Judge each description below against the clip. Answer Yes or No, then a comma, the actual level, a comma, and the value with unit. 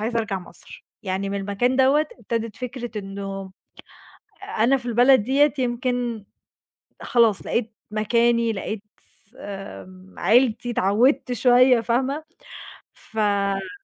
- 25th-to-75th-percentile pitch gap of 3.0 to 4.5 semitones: Yes, average, 3.8 semitones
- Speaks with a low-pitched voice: No, high, 230 Hz